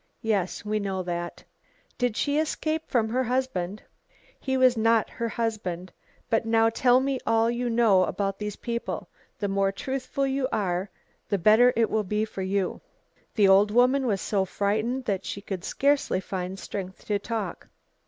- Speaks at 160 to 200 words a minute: Yes, average, 170 wpm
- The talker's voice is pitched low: No, high, 220 Hz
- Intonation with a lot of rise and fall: No, average, 4.0 semitones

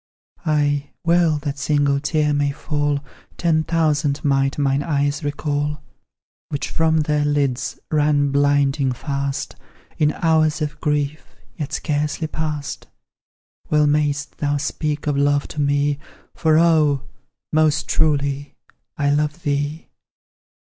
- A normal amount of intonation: No, narrow, 1.2 semitones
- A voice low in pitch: No, medium, 145 Hz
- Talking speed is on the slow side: Yes, slow, 120 wpm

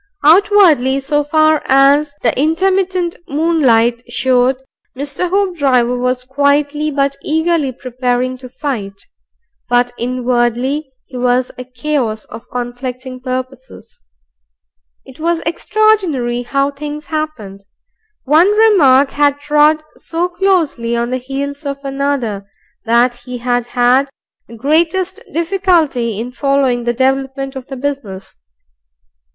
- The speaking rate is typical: No, slow, 115 wpm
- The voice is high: Yes, very high, 275 Hz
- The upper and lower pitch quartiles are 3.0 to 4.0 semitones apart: Yes, average, 3.6 semitones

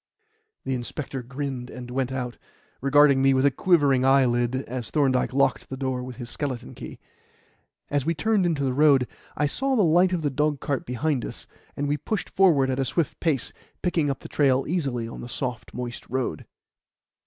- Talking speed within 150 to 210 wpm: Yes, average, 190 wpm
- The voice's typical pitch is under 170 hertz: Yes, low, 135 Hz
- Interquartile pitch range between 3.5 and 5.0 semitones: No, average, 2.8 semitones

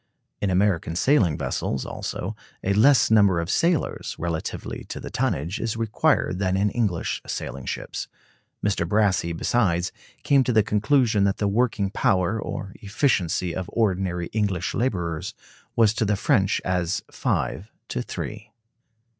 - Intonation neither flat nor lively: Yes, average, 3.7 semitones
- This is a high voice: No, low, 100 Hz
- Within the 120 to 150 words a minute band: Yes, average, 145 wpm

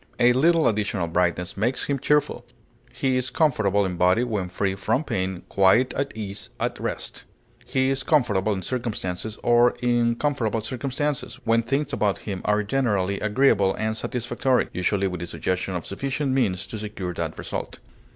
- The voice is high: No, low, 110 Hz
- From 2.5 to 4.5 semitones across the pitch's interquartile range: No, average, 5.0 semitones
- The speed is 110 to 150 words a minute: No, average, 165 wpm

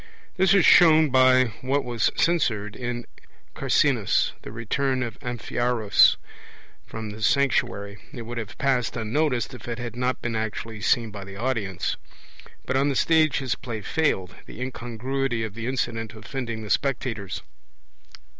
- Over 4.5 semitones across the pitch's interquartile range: No, average, 3.2 semitones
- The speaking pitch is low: Yes, low, 120 Hz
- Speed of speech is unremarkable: Yes, average, 150 wpm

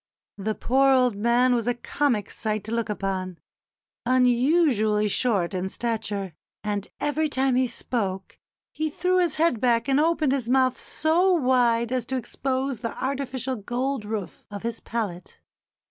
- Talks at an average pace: Yes, average, 155 wpm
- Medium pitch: No, high, 245 Hz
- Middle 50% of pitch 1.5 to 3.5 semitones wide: No, average, 3.9 semitones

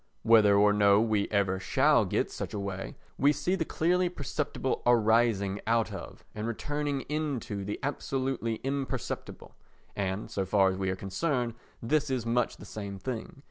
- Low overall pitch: Yes, low, 115 Hz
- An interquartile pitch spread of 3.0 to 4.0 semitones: No, wide, 5.4 semitones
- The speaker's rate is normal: Yes, average, 165 wpm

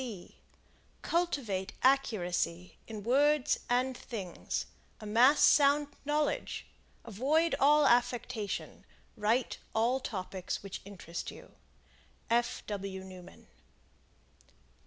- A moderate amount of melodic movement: No, wide, 5.9 semitones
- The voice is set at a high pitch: Yes, high, 235 Hz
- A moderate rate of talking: No, slow, 85 wpm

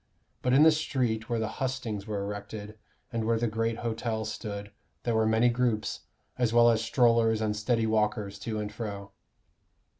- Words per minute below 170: No, average, 175 wpm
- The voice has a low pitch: Yes, low, 110 Hz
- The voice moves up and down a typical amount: No, narrow, 1.8 semitones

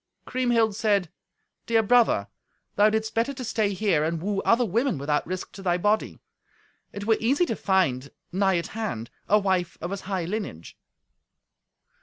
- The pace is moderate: Yes, average, 165 wpm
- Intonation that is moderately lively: Yes, average, 3.9 semitones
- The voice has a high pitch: Yes, high, 205 Hz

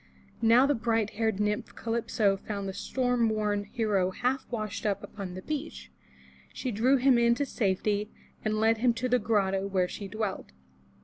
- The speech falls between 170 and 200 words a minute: Yes, average, 175 wpm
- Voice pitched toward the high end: Yes, high, 220 Hz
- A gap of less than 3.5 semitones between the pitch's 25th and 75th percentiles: Yes, average, 2.9 semitones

